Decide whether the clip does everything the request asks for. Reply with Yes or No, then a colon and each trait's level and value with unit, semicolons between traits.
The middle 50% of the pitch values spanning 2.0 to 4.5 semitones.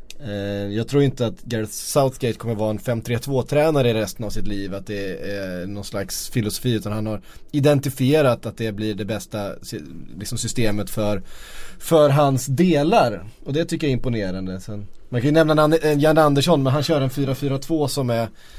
No: average, 5.3 semitones